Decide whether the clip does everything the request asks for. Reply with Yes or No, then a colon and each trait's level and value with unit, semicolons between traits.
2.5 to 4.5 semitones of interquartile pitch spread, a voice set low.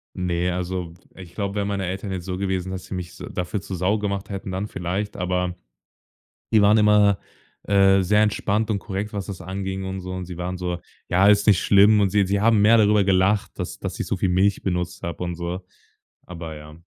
No: narrow, 2.1 semitones; very low, 95 Hz